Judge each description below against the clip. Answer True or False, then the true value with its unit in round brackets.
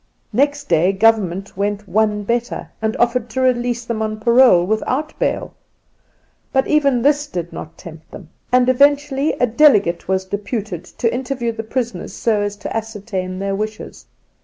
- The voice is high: True (225 Hz)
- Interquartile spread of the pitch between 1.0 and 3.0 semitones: False (4.1 semitones)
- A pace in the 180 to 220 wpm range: False (160 wpm)